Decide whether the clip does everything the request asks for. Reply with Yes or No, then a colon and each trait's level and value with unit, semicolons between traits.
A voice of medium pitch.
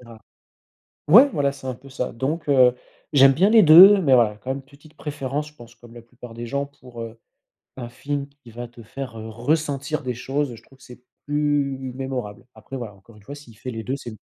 No: low, 130 Hz